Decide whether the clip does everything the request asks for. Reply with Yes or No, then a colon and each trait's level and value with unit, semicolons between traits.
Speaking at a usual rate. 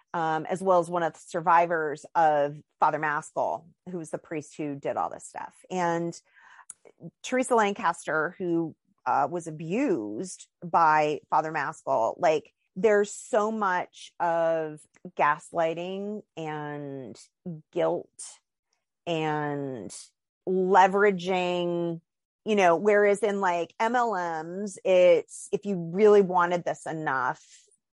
No: slow, 115 wpm